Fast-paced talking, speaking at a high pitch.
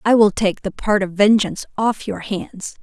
Yes: fast, 210 wpm; high, 205 Hz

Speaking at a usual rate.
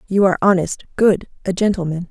Yes: average, 170 wpm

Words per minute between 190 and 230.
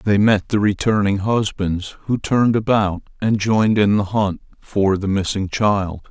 No: average, 165 wpm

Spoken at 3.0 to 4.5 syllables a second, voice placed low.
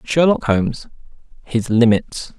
Yes: 4.0 syllables/s; low, 120 Hz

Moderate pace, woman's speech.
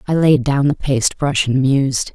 No: fast, 225 wpm; female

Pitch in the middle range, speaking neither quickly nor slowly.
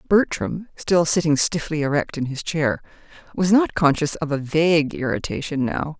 Yes: medium, 155 Hz; average, 160 wpm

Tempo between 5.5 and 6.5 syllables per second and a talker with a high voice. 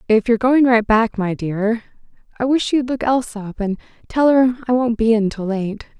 No: 5.1 syllables/s; high, 230 Hz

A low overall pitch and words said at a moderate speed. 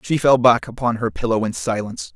No: low, 115 Hz; fast, 225 wpm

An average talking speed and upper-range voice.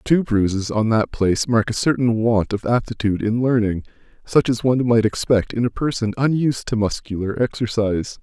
No: average, 180 wpm; low, 115 Hz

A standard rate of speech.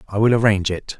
No: fast, 240 wpm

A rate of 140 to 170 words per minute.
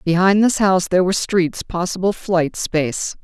Yes: average, 165 wpm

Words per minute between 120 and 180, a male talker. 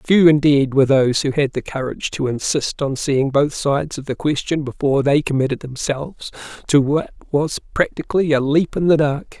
No: average, 190 wpm; male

